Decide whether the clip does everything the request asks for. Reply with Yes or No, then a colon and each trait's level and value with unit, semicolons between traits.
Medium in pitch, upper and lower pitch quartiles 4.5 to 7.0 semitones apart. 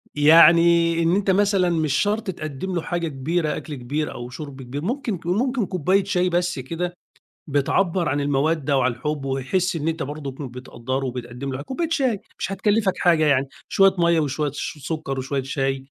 Yes: medium, 160 Hz; average, 4.8 semitones